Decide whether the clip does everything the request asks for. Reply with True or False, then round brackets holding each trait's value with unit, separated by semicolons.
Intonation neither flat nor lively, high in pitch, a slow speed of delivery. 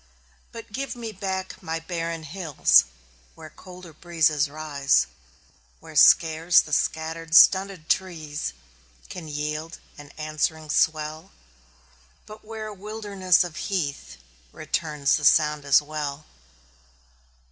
False (3.5 semitones; 160 Hz; 115 wpm)